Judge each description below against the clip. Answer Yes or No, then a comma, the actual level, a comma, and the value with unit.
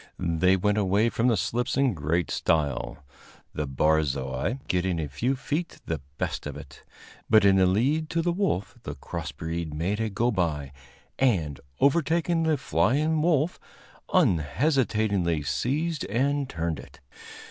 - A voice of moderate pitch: No, low, 100 Hz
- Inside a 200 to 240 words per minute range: No, average, 150 wpm